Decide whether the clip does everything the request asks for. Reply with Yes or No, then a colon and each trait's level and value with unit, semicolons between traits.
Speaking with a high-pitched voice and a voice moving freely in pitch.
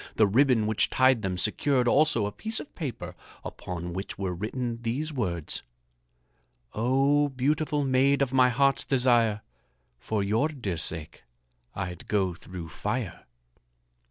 No: low, 120 Hz; wide, 6.0 semitones